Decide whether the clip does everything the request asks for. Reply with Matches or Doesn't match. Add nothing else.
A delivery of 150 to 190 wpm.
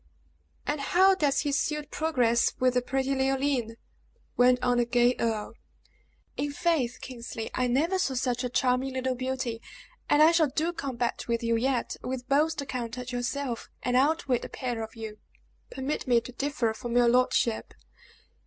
Matches